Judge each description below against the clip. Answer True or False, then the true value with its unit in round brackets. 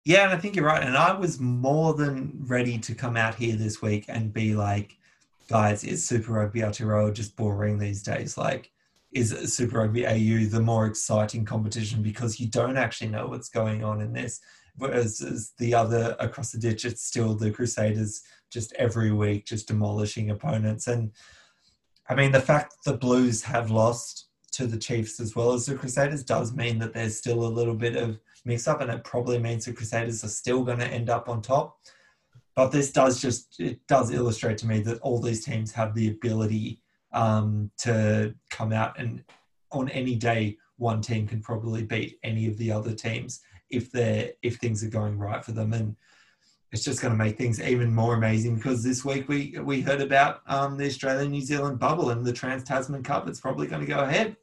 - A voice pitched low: True (115 Hz)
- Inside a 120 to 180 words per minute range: False (200 wpm)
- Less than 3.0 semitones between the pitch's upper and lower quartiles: True (2.4 semitones)